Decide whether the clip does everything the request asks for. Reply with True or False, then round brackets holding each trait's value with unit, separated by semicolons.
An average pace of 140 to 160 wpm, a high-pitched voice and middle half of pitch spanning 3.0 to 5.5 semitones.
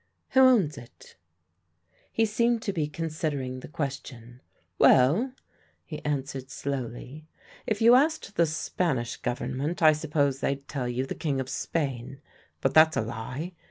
False (145 wpm; 145 Hz; 4.4 semitones)